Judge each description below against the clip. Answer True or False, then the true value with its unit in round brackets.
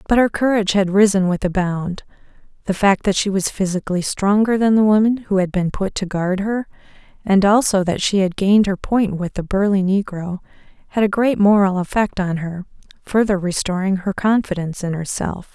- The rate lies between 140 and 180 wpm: False (195 wpm)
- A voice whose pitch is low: False (195 Hz)